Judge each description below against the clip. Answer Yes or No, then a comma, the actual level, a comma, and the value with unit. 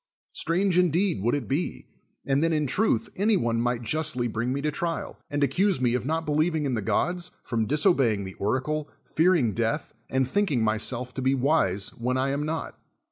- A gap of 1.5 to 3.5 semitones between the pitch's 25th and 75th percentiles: No, average, 5.1 semitones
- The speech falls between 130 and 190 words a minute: No, average, 200 wpm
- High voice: No, medium, 140 Hz